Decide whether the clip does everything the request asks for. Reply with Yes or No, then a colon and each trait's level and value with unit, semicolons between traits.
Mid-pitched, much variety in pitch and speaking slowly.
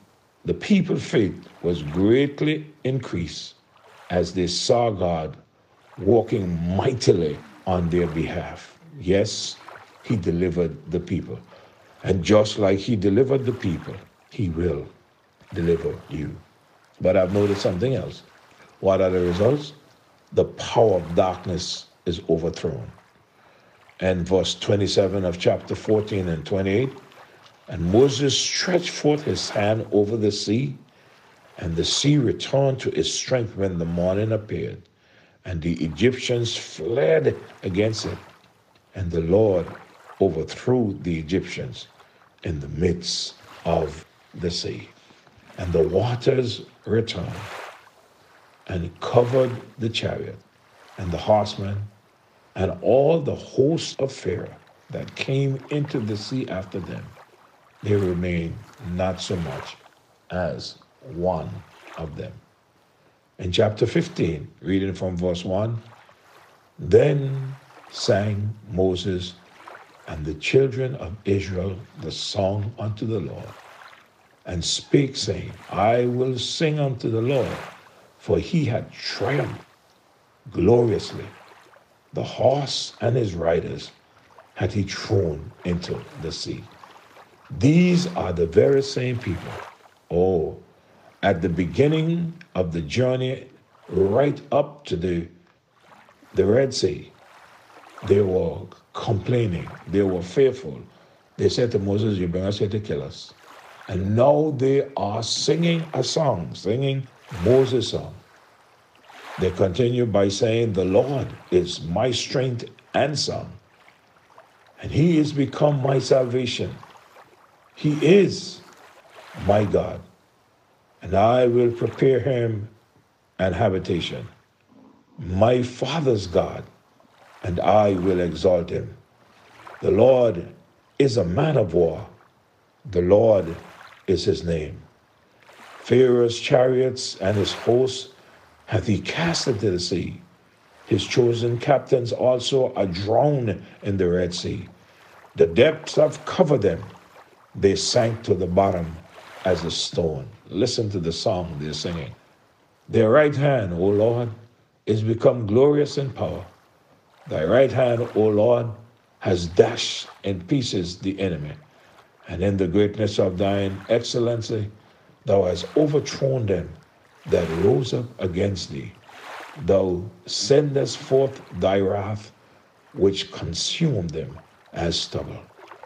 No: low, 110 Hz; wide, 5.7 semitones; slow, 120 wpm